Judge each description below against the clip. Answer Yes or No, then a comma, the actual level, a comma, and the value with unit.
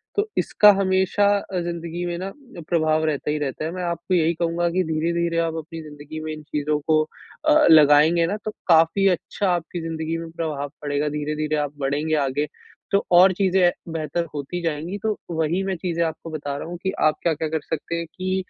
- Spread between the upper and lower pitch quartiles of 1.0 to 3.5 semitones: Yes, narrow, 2.4 semitones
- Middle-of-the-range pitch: Yes, medium, 165 Hz